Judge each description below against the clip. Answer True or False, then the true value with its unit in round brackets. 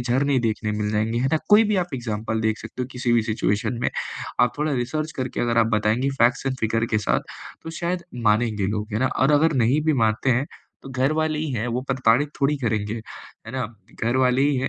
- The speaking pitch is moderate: False (125 Hz)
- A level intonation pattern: False (3.7 semitones)